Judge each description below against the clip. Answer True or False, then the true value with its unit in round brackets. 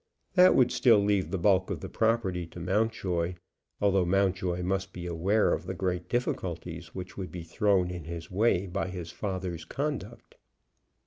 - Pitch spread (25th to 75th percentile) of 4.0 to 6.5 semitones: False (2.5 semitones)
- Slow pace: False (170 wpm)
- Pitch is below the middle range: True (95 Hz)